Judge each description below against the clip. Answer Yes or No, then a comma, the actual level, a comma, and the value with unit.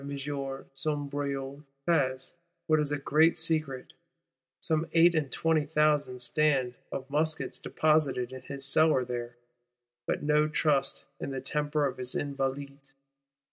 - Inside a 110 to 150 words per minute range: Yes, average, 140 wpm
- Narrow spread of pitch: Yes, narrow, 2.2 semitones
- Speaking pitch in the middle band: Yes, medium, 145 Hz